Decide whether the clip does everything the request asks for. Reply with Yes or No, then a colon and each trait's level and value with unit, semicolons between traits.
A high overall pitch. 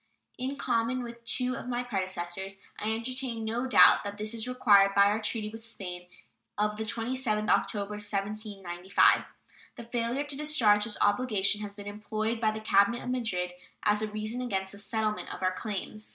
Yes: high, 215 Hz